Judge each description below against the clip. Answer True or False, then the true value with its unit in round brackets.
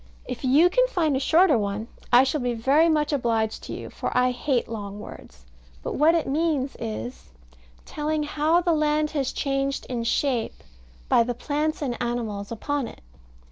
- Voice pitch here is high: True (270 Hz)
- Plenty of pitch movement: False (4.7 semitones)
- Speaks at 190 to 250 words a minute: False (180 wpm)